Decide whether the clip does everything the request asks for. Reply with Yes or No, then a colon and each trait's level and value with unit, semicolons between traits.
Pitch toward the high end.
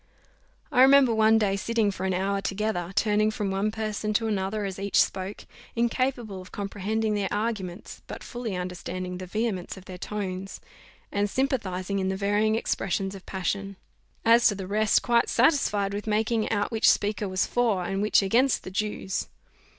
Yes: high, 205 Hz